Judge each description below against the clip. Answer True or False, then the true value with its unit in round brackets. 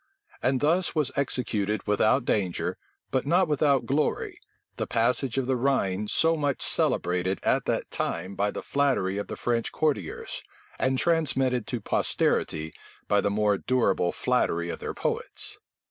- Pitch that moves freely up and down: True (5.7 semitones)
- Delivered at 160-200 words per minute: False (150 wpm)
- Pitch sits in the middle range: False (125 Hz)